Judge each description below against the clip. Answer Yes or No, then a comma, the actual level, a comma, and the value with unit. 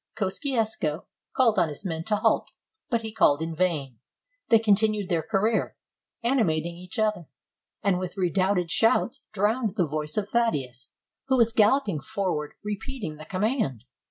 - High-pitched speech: Yes, high, 195 Hz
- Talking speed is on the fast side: No, average, 155 wpm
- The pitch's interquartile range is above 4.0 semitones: Yes, wide, 5.4 semitones